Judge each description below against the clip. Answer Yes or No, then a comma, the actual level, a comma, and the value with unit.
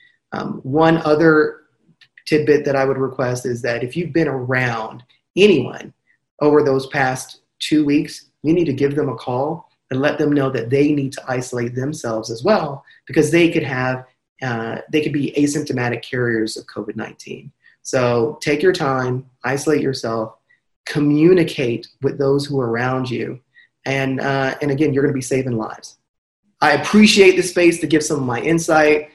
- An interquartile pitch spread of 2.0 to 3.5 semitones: Yes, average, 3.2 semitones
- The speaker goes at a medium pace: Yes, average, 175 wpm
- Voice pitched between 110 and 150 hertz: Yes, medium, 140 Hz